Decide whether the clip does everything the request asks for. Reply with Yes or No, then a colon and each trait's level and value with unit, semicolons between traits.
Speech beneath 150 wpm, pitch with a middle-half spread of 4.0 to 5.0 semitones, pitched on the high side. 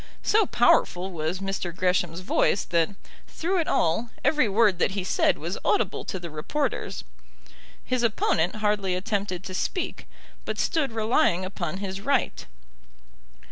Yes: average, 140 wpm; average, 4.3 semitones; high, 195 Hz